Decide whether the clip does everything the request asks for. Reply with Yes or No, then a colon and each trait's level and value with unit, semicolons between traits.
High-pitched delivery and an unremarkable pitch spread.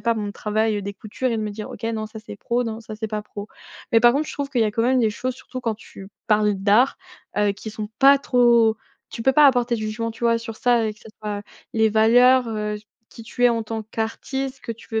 No: high, 225 Hz; narrow, 2.2 semitones